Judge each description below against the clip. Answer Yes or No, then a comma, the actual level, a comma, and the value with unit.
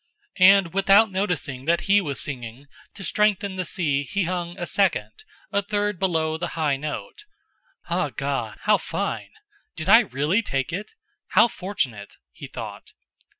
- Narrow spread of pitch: No, average, 5.1 semitones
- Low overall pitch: No, medium, 180 Hz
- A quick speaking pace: No, average, 150 wpm